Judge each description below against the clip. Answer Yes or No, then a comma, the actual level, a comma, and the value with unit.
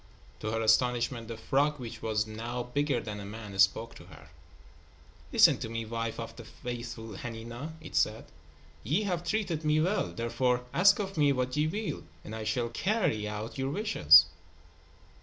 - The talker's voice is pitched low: Yes, low, 120 Hz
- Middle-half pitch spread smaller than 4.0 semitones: No, average, 5.1 semitones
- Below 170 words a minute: No, average, 175 wpm